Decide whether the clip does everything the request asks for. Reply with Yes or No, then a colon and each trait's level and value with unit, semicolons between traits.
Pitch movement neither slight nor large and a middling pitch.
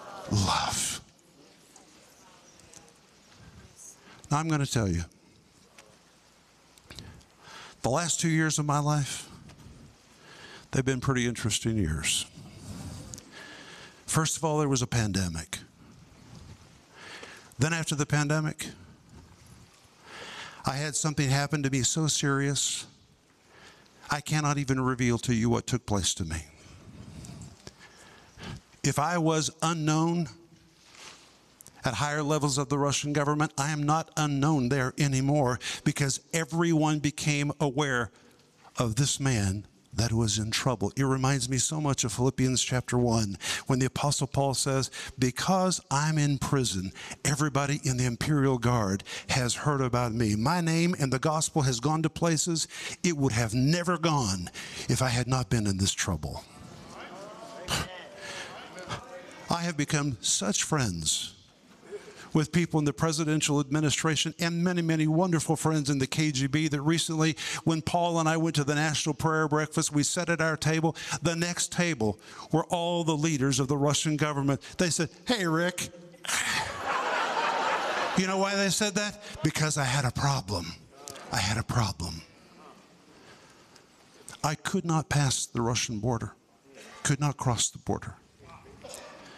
Yes: average, 4.1 semitones; medium, 145 Hz